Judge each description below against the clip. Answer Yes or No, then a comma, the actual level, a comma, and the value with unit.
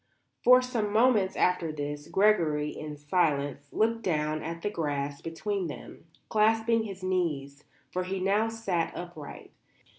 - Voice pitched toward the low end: No, medium, 180 Hz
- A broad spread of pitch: Yes, wide, 5.9 semitones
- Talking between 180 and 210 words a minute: No, average, 140 wpm